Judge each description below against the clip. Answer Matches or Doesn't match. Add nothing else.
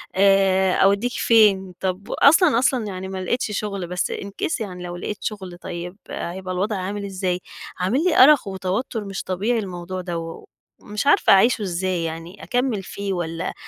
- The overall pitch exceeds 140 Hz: Matches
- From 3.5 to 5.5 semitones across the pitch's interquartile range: Doesn't match